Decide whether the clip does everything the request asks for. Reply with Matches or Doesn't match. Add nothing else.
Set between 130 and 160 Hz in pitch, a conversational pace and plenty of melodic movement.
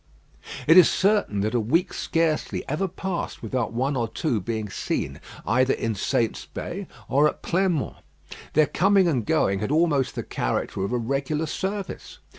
Matches